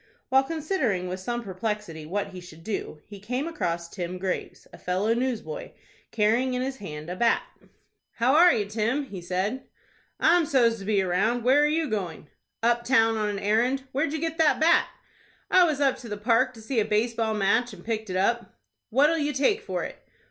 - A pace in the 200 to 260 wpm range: Yes, fast, 205 wpm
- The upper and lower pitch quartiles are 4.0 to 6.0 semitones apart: Yes, average, 5.3 semitones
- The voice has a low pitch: No, high, 230 Hz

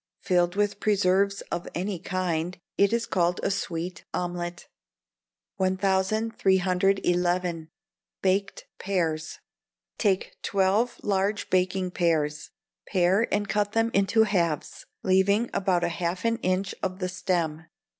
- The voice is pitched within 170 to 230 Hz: Yes, medium, 185 Hz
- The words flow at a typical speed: No, slow, 115 wpm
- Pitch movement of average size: No, narrow, 2.2 semitones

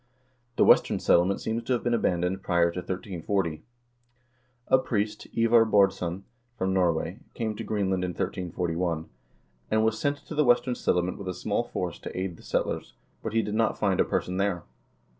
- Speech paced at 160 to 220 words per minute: Yes, average, 180 wpm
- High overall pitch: No, very low, 95 Hz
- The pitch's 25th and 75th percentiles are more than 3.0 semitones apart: Yes, average, 3.7 semitones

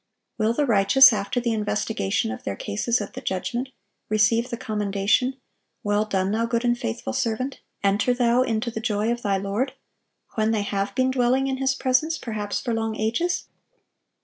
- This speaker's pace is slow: No, average, 175 wpm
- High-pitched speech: Yes, high, 225 Hz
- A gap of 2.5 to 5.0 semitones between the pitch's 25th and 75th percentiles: Yes, average, 3.4 semitones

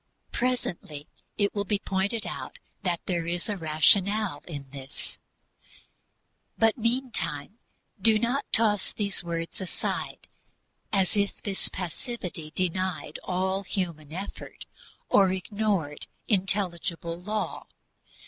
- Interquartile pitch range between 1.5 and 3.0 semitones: No, average, 3.7 semitones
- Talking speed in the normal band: No, slow, 110 wpm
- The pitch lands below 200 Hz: Yes, high, 190 Hz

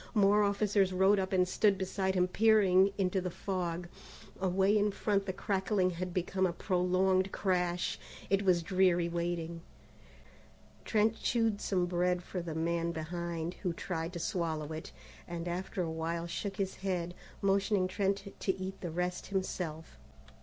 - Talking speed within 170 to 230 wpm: No, average, 155 wpm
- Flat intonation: Yes, narrow, 2.3 semitones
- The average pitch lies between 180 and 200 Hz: Yes, medium, 185 Hz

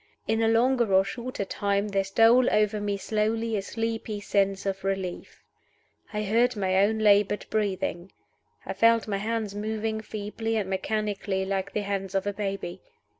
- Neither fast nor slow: Yes, average, 165 wpm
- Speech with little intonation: Yes, narrow, 2.2 semitones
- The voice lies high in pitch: Yes, high, 205 Hz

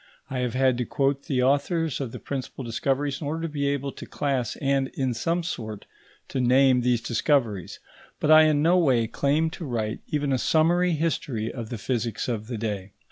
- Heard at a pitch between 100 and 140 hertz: Yes, low, 135 Hz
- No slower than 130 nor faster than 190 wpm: No, average, 200 wpm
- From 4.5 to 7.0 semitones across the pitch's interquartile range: No, average, 3.7 semitones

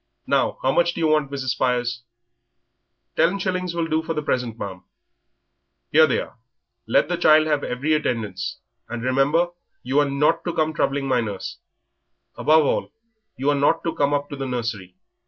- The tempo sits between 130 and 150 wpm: No, average, 180 wpm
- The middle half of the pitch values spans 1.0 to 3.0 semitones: No, average, 4.1 semitones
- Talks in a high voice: No, medium, 140 Hz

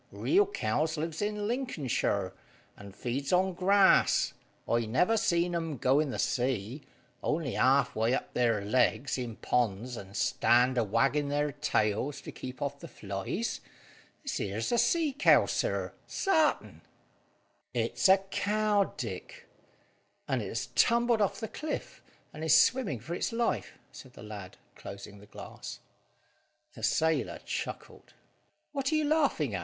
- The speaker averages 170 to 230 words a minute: No, average, 150 wpm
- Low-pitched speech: No, medium, 150 Hz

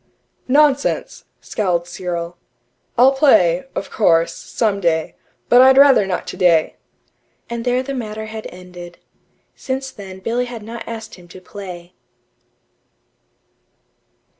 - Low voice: No, high, 210 Hz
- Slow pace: Yes, slow, 120 wpm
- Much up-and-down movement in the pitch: Yes, wide, 5.8 semitones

